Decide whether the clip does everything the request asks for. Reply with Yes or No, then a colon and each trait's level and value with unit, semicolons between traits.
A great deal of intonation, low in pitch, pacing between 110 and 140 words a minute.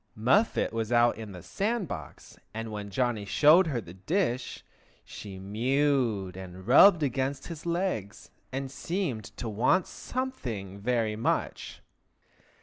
Yes: wide, 6.5 semitones; low, 120 Hz; slow, 135 wpm